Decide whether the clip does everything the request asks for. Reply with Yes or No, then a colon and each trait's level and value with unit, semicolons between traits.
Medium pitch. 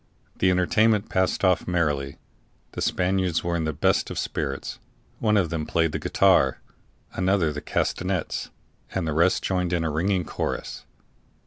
No: very low, 90 Hz